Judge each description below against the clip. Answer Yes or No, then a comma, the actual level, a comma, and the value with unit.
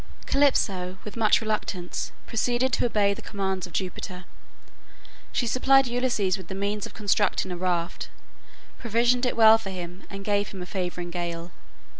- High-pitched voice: Yes, high, 200 Hz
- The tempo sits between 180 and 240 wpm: No, average, 160 wpm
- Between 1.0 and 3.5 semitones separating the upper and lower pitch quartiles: No, average, 4.0 semitones